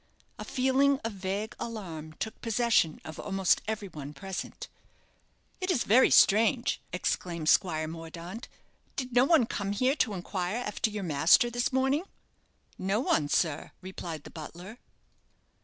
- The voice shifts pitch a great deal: Yes, wide, 6.0 semitones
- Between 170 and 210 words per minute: No, average, 140 wpm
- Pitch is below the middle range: No, high, 200 Hz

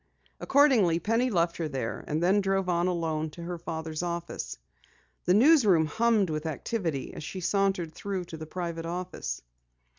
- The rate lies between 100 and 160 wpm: No, average, 170 wpm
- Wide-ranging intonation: No, average, 3.5 semitones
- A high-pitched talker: No, medium, 175 Hz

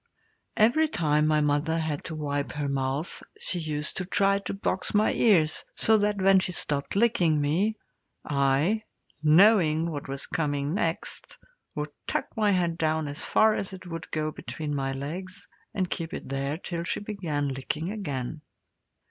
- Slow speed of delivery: No, average, 165 wpm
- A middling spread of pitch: Yes, average, 4.5 semitones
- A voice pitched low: No, medium, 160 Hz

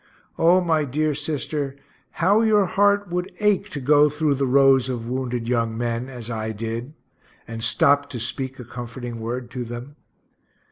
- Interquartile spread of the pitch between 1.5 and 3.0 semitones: No, average, 4.3 semitones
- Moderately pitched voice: No, low, 130 Hz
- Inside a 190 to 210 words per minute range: No, average, 170 wpm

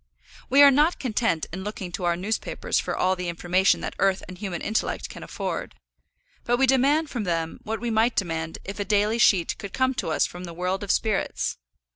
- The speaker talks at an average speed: No, fast, 210 wpm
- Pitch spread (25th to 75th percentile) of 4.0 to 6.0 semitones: Yes, average, 4.8 semitones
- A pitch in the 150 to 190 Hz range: No, high, 200 Hz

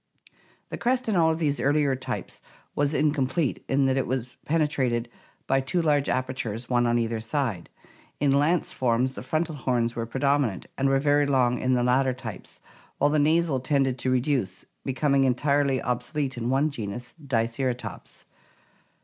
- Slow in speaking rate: No, average, 165 wpm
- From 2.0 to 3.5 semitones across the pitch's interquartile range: Yes, average, 2.8 semitones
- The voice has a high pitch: No, low, 135 Hz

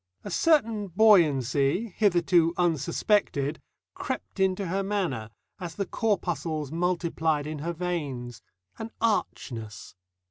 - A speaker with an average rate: No, slow, 105 wpm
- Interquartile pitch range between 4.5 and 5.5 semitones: Yes, average, 5.1 semitones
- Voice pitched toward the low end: No, medium, 170 Hz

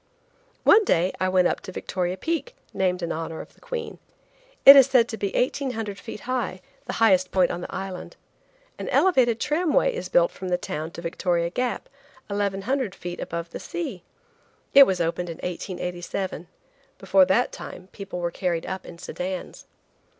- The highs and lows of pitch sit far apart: Yes, wide, 5.7 semitones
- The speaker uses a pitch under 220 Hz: Yes, high, 190 Hz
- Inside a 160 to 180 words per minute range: Yes, average, 170 wpm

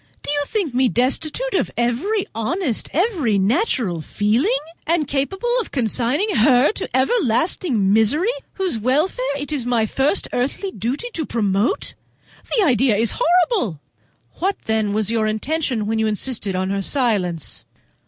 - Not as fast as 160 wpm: Yes, average, 150 wpm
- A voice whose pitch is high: Yes, very high, 255 Hz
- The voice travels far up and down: Yes, wide, 7.3 semitones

